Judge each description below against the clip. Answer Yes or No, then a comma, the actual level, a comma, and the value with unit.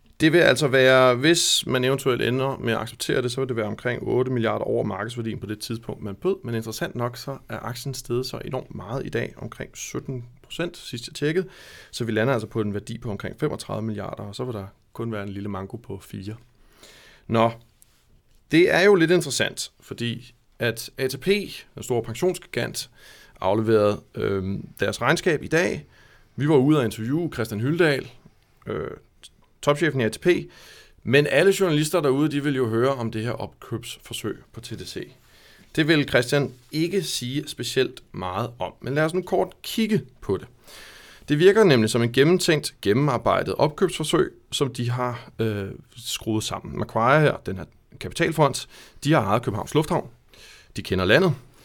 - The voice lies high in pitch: No, low, 125 Hz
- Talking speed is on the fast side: No, average, 175 wpm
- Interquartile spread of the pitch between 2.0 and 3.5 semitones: No, average, 4.8 semitones